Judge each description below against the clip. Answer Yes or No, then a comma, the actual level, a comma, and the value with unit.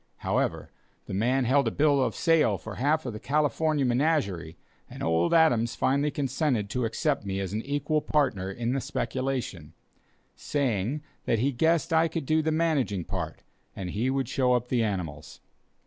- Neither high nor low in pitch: No, low, 130 Hz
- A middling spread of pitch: No, wide, 6.0 semitones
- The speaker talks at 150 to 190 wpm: Yes, average, 175 wpm